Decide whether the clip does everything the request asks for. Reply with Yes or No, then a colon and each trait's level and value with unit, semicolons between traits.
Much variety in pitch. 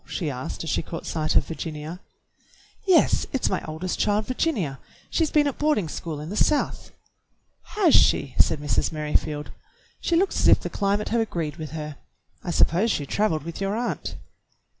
Yes: wide, 6.8 semitones